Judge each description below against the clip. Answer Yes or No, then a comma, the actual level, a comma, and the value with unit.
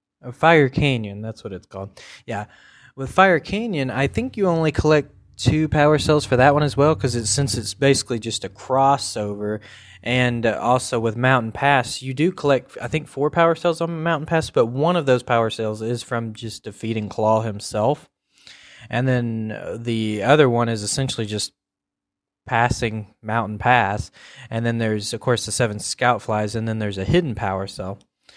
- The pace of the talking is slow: No, average, 180 wpm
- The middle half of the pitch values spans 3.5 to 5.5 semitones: Yes, average, 4.6 semitones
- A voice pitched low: Yes, low, 120 Hz